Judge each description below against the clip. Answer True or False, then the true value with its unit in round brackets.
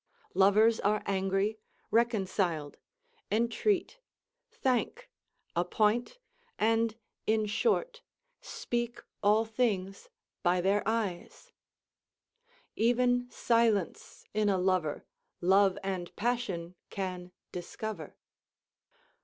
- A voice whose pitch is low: False (210 Hz)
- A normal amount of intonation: True (3.7 semitones)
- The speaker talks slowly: True (80 wpm)